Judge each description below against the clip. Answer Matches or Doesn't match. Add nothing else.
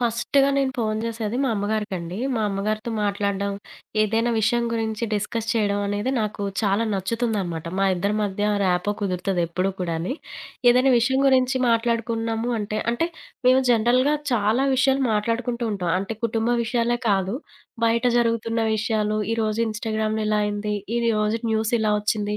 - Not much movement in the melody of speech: Matches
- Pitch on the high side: Matches